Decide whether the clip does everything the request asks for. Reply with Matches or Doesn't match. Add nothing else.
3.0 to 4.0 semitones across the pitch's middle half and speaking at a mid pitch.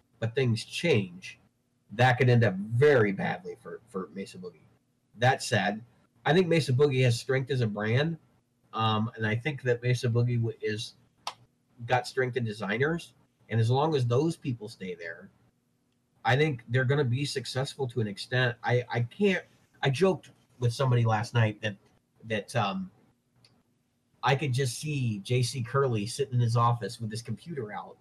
Doesn't match